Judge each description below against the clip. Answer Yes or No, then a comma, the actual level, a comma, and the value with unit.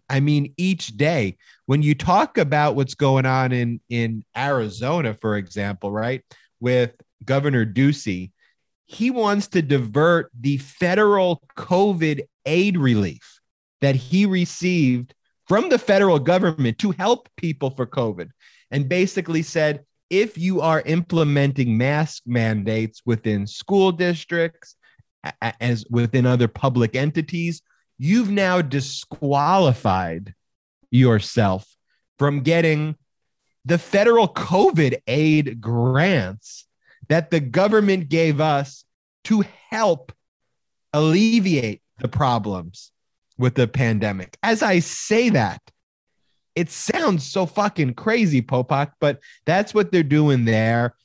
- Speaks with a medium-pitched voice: Yes, medium, 145 Hz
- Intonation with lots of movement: Yes, wide, 6.2 semitones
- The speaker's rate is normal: No, slow, 115 wpm